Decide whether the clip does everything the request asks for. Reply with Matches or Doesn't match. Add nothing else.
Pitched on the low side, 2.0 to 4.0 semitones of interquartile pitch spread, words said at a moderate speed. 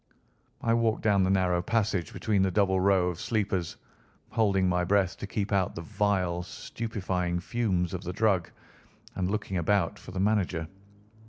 Matches